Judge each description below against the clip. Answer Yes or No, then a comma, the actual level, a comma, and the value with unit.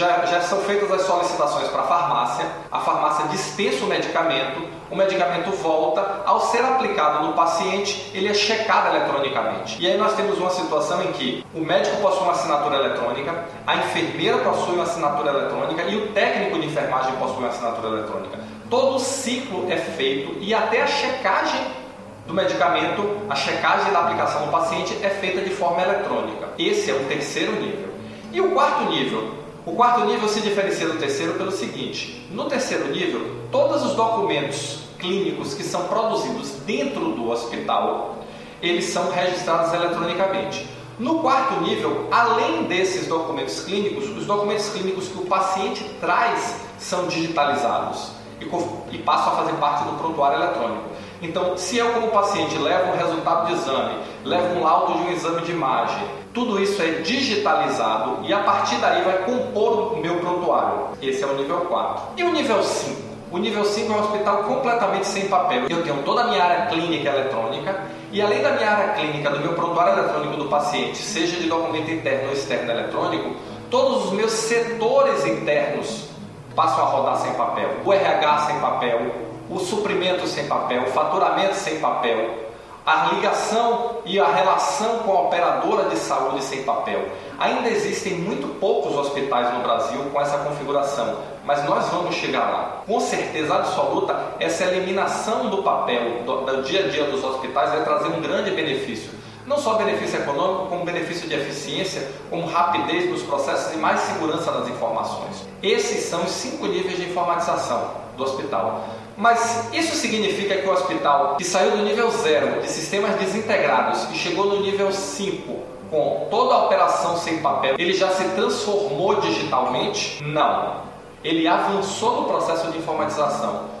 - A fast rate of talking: No, average, 165 wpm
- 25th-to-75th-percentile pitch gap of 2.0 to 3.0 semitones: No, wide, 5.4 semitones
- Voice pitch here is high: No, medium, 175 Hz